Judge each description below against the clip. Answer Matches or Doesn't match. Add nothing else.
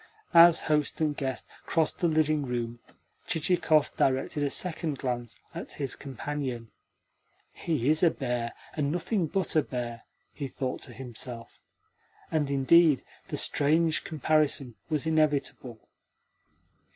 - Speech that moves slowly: Matches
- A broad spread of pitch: Doesn't match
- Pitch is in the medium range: Matches